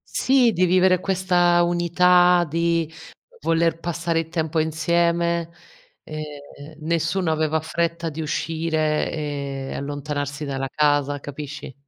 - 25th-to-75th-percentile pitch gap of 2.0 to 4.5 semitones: Yes, narrow, 2.4 semitones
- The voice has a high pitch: No, medium, 160 Hz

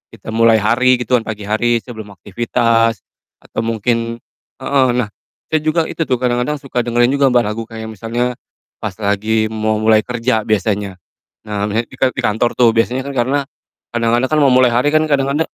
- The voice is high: No, low, 115 Hz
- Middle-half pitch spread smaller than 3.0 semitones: Yes, narrow, 2.6 semitones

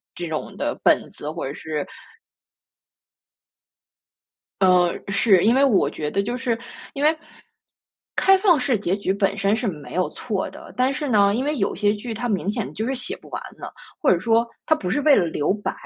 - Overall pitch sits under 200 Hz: No, high, 210 Hz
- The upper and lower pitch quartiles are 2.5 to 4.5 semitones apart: No, average, 5.3 semitones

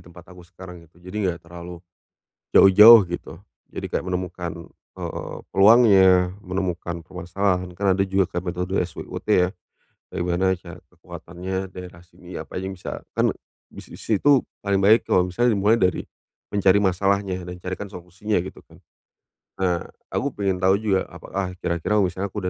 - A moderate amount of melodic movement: No, narrow, 1.7 semitones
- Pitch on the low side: Yes, very low, 95 Hz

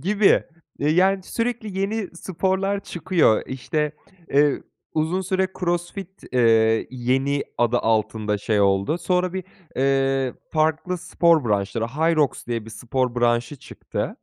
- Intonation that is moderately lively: No, wide, 7.3 semitones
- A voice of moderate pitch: Yes, medium, 145 Hz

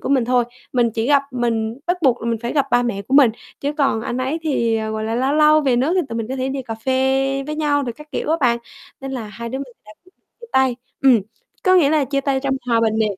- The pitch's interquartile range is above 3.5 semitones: No, average, 3.2 semitones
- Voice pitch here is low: No, very high, 260 Hz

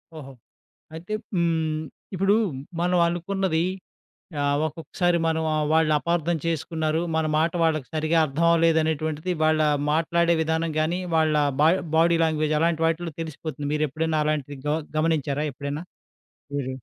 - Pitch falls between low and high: Yes, medium, 160 Hz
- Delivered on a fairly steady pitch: Yes, narrow, 1.5 semitones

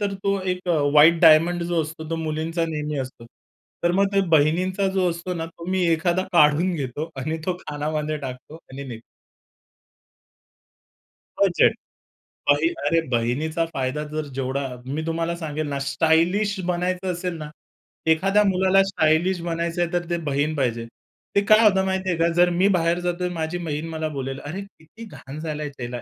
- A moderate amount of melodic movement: Yes, average, 3.1 semitones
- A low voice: No, medium, 165 Hz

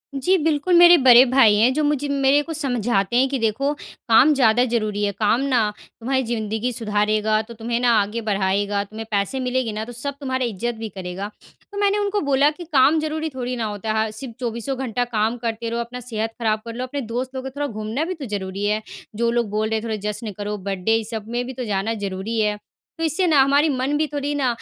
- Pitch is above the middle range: Yes, high, 235 Hz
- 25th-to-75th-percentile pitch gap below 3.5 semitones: No, average, 4.0 semitones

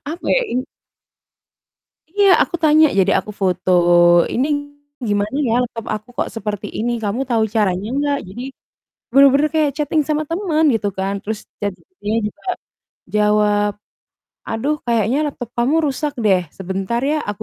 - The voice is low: No, high, 230 Hz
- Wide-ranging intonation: Yes, wide, 6.0 semitones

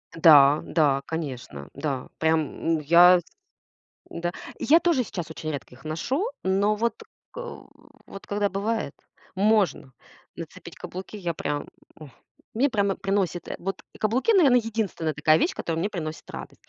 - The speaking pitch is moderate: Yes, medium, 175 Hz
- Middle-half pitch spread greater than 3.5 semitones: Yes, wide, 5.4 semitones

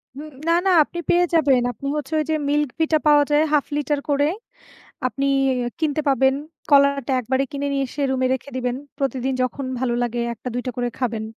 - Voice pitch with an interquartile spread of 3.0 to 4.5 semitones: No, narrow, 2.5 semitones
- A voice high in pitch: Yes, very high, 275 Hz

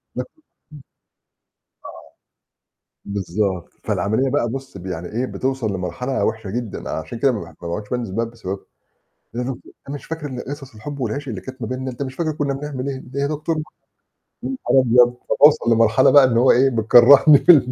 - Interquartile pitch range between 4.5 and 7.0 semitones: No, average, 3.8 semitones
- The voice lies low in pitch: Yes, low, 125 Hz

